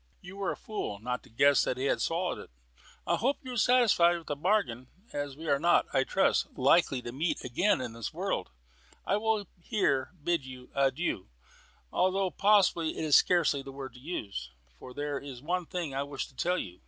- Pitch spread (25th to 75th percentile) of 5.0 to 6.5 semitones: Yes, wide, 5.5 semitones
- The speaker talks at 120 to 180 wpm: No, fast, 205 wpm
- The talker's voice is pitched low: No, medium, 150 Hz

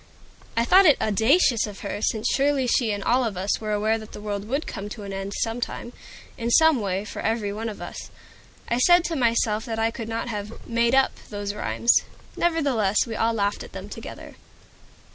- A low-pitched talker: No, high, 225 Hz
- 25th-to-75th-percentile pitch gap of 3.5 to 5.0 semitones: No, average, 2.8 semitones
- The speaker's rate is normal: No, fast, 210 wpm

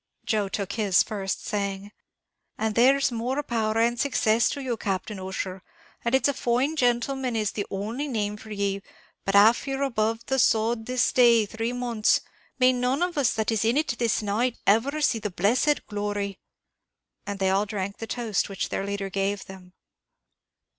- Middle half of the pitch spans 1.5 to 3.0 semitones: No, average, 3.5 semitones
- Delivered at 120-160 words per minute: No, average, 180 wpm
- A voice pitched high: Yes, high, 220 Hz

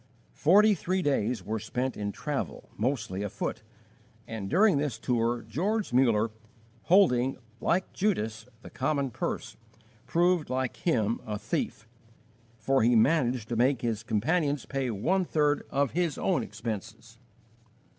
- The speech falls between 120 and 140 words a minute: Yes, slow, 135 wpm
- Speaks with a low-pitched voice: Yes, low, 125 Hz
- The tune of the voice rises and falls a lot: Yes, wide, 5.8 semitones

